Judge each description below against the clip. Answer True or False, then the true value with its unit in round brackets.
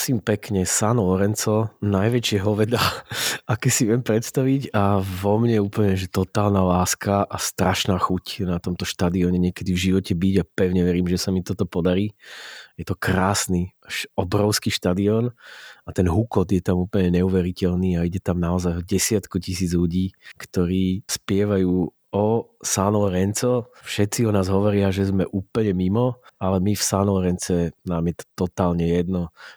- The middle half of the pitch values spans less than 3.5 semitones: True (2.5 semitones)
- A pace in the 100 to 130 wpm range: False (155 wpm)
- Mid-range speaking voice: False (95 Hz)